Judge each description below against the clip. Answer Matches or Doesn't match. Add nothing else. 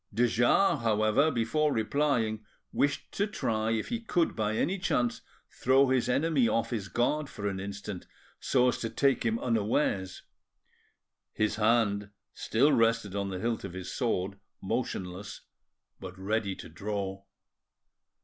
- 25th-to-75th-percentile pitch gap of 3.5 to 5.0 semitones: Matches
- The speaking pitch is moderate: Doesn't match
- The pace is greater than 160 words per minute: Doesn't match